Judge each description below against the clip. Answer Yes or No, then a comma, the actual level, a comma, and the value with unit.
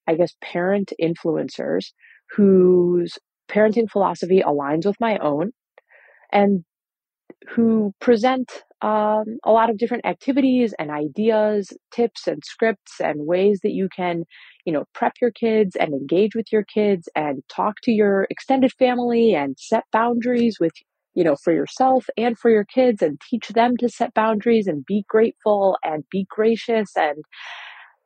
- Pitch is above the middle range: Yes, high, 215 Hz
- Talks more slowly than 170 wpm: Yes, average, 150 wpm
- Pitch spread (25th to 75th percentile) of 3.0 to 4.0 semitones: Yes, average, 3.7 semitones